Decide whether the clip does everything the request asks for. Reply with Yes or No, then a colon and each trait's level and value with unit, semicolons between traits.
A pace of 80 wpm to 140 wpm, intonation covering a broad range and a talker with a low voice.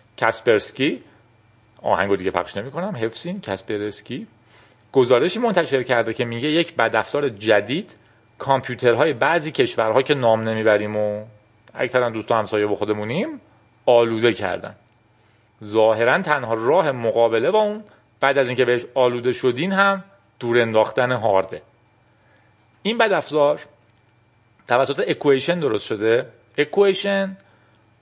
No: average, 110 wpm; average, 5.0 semitones; low, 120 Hz